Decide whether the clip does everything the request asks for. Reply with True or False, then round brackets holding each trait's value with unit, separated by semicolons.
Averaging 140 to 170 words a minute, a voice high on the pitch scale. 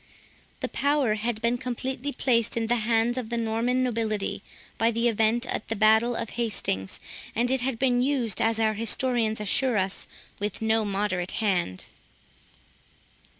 True (155 wpm; 230 Hz)